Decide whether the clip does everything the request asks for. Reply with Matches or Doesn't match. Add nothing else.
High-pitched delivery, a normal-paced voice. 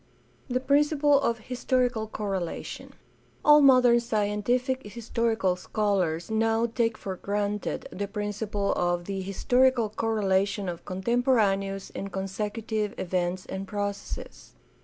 Doesn't match